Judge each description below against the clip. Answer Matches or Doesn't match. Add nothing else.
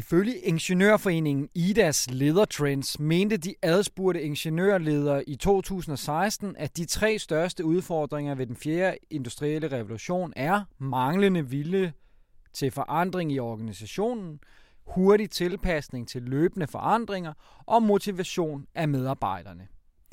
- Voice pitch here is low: Doesn't match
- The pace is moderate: Doesn't match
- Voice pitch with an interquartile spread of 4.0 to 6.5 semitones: Matches